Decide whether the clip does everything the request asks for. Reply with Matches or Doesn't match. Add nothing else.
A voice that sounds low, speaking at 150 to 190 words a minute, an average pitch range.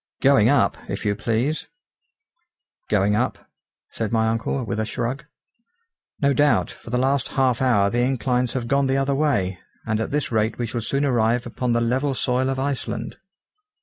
Matches